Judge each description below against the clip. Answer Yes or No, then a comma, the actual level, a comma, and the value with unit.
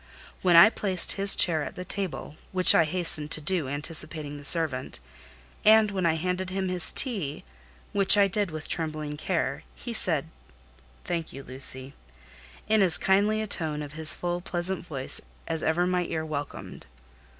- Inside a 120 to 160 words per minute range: No, average, 170 wpm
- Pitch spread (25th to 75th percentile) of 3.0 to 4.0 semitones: Yes, average, 3.7 semitones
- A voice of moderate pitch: Yes, medium, 170 Hz